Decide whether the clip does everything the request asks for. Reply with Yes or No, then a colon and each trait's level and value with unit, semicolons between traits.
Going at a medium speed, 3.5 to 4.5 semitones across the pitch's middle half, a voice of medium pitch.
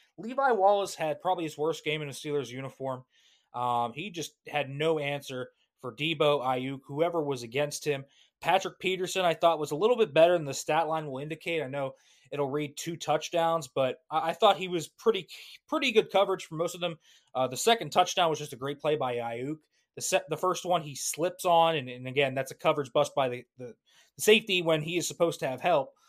No: fast, 220 wpm; average, 4.0 semitones; medium, 155 Hz